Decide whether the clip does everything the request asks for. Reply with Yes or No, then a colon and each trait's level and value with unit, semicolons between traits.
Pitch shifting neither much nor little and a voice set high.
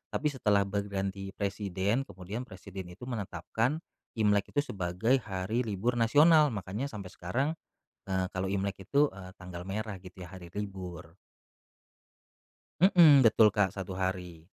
No: average, 3.4 semitones; low, 100 Hz